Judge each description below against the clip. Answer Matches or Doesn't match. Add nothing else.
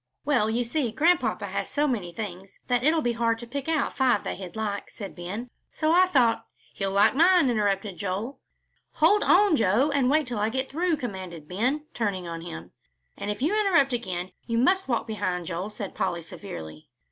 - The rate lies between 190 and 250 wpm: Matches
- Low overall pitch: Doesn't match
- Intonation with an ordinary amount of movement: Doesn't match